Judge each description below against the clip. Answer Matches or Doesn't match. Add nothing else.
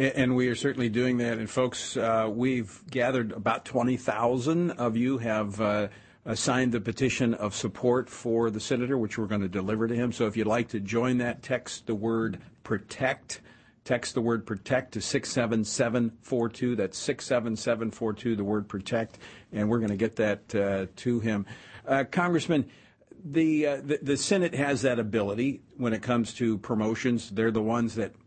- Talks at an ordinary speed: Matches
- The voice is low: Matches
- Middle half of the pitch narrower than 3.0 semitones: Matches